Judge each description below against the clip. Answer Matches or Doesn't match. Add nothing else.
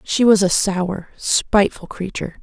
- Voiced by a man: Doesn't match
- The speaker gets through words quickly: Doesn't match